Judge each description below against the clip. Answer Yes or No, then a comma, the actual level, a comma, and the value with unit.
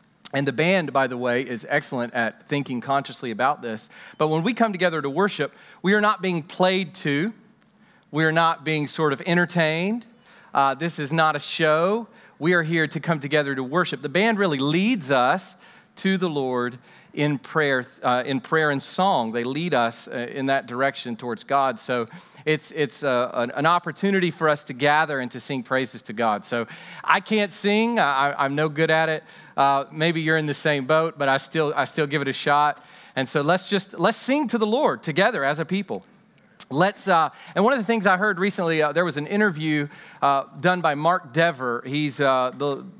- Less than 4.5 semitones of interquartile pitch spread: No, average, 4.8 semitones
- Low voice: No, medium, 155 Hz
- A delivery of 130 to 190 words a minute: No, fast, 205 wpm